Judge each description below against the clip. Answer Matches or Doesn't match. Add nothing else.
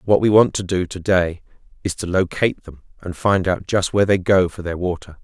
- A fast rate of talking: Matches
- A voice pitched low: Matches